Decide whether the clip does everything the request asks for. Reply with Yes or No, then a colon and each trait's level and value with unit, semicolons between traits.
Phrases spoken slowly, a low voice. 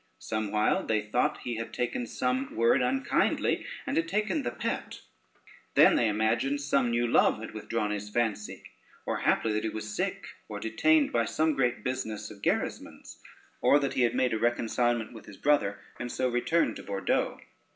No: average, 180 wpm; low, 120 Hz